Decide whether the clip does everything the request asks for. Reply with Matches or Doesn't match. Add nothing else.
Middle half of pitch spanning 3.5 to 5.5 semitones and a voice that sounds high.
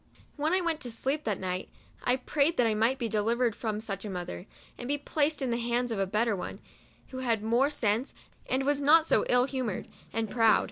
Matches